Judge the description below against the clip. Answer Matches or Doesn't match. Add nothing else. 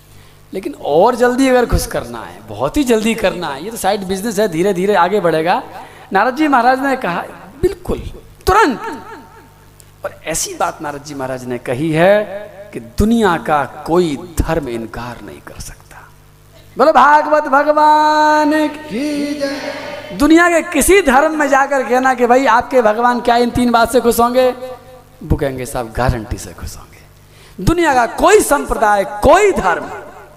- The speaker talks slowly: Doesn't match